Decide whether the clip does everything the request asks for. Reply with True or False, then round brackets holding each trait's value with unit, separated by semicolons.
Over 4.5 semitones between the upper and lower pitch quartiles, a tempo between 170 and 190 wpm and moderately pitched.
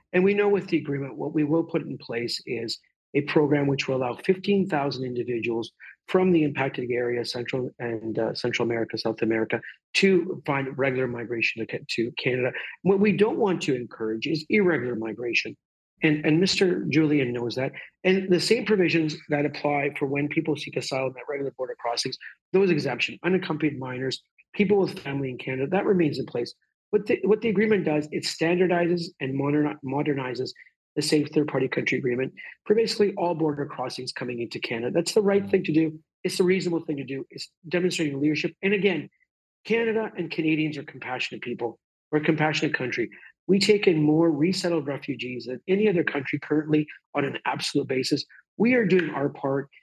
True (5.3 semitones; 185 wpm; 150 Hz)